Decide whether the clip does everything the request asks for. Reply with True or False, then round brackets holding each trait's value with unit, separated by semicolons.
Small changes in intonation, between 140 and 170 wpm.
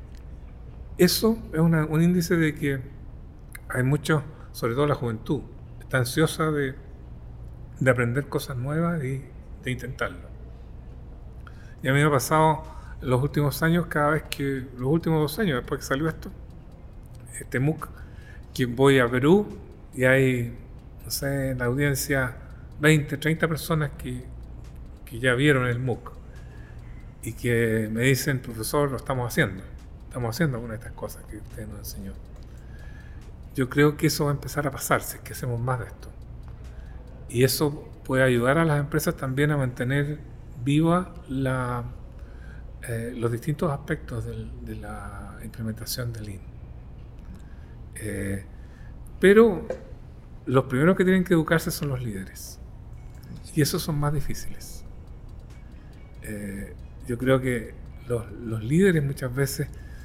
False (5.5 semitones; 145 wpm)